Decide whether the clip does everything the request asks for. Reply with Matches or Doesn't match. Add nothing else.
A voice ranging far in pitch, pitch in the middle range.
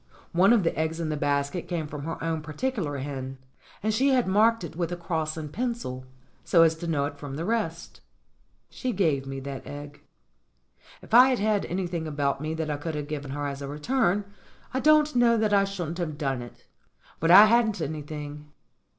Matches